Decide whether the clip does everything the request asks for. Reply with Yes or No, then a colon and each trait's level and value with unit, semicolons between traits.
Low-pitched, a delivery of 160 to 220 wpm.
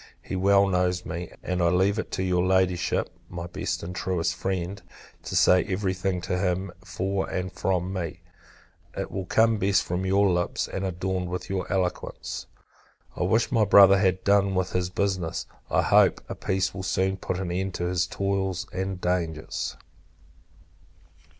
Yes: very low, 95 Hz; average, 170 wpm